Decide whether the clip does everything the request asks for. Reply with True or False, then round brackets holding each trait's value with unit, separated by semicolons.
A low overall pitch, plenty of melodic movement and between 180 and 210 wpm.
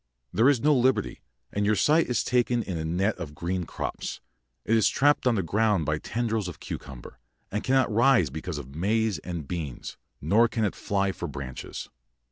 True (100 Hz; 6.0 semitones; 190 wpm)